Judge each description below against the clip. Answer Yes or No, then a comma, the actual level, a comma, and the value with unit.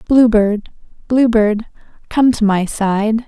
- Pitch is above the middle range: Yes, high, 220 Hz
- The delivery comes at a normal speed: Yes, average, 145 wpm